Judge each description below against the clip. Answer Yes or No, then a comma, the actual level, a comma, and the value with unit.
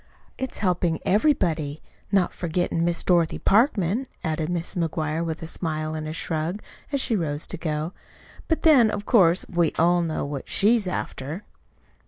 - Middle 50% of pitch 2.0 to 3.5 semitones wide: No, average, 3.9 semitones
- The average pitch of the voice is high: No, medium, 170 Hz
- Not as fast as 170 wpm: Yes, average, 160 wpm